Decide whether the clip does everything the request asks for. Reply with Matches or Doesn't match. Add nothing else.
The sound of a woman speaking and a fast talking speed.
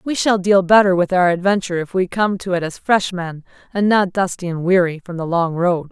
Matches